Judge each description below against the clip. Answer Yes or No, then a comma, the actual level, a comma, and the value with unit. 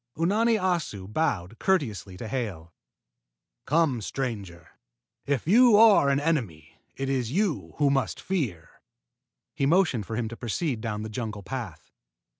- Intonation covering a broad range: Yes, wide, 7.8 semitones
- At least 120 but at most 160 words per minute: Yes, average, 140 wpm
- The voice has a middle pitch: No, low, 130 Hz